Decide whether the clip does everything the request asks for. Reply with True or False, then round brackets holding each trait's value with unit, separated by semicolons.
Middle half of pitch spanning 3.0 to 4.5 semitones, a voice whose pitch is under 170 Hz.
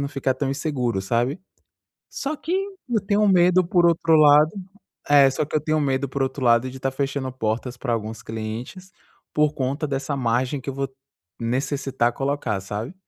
True (3.7 semitones; 135 Hz)